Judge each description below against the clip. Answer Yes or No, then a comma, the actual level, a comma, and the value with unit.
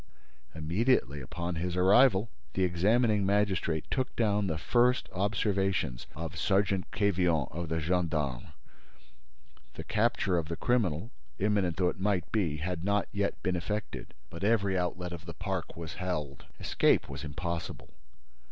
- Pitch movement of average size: Yes, average, 3.6 semitones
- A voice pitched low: Yes, very low, 90 Hz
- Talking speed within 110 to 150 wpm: Yes, average, 145 wpm